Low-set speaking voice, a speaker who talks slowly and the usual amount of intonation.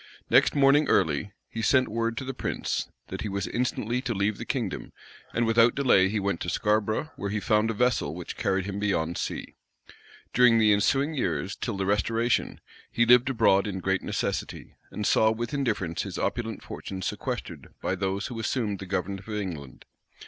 No: low, 105 Hz; average, 185 wpm; average, 3.4 semitones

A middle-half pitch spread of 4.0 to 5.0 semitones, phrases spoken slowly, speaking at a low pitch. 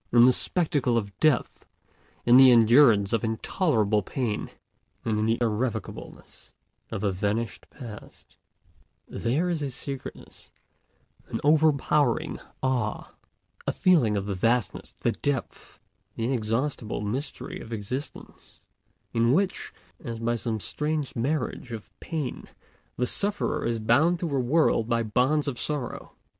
Yes: average, 4.4 semitones; slow, 130 wpm; low, 120 Hz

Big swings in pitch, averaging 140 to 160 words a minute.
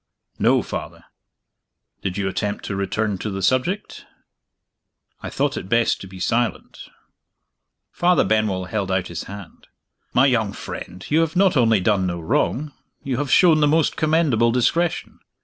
Yes: wide, 7.1 semitones; average, 155 wpm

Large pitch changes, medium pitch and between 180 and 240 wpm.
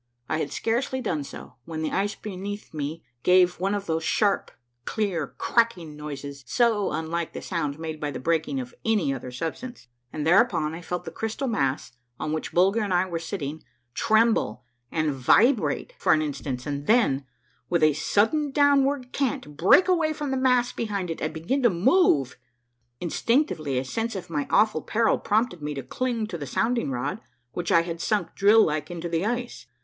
Yes: wide, 6.8 semitones; medium, 175 Hz; average, 185 wpm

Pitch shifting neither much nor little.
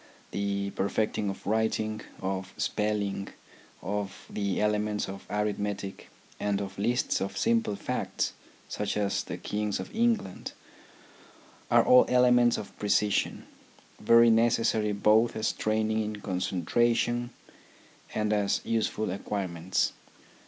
No: narrow, 1.9 semitones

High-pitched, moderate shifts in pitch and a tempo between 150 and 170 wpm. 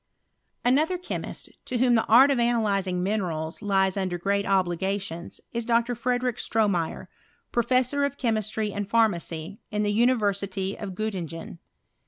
No: high, 210 Hz; average, 3.8 semitones; slow, 135 wpm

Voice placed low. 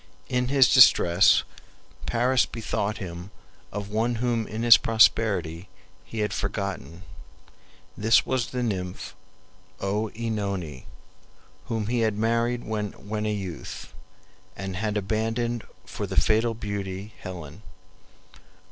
Yes: low, 110 Hz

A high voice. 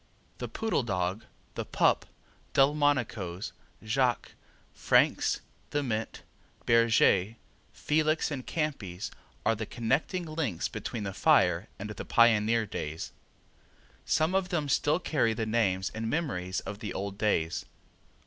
No: low, 115 Hz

